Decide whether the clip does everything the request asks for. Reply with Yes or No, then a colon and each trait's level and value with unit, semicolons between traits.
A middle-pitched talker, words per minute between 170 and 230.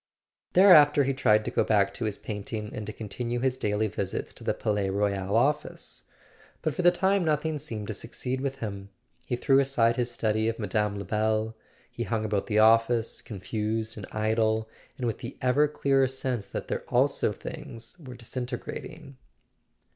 No: low, 115 Hz; average, 175 wpm